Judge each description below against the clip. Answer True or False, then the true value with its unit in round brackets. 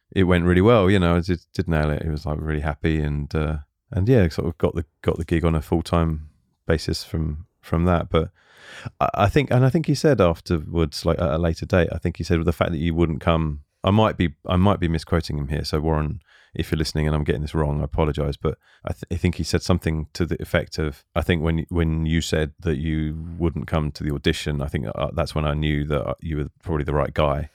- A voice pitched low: True (80 Hz)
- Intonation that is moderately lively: False (2.3 semitones)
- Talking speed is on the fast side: True (265 wpm)